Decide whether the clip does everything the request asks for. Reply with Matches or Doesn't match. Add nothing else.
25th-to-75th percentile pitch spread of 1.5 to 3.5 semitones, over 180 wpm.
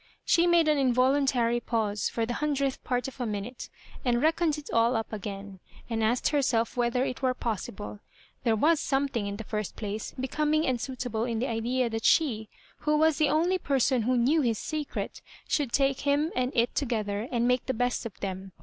Doesn't match